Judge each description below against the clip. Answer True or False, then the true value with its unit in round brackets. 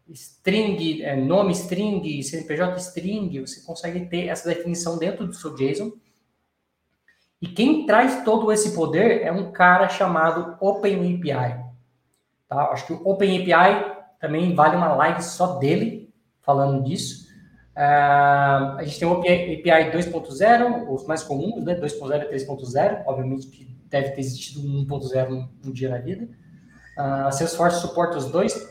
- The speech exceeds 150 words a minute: False (145 wpm)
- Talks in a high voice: False (165 Hz)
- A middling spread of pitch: True (4.7 semitones)